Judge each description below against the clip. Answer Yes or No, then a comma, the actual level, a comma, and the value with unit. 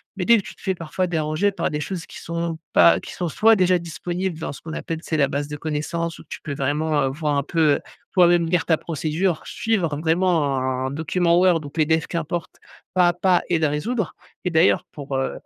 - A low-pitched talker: No, medium, 165 Hz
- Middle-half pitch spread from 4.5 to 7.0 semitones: No, average, 2.8 semitones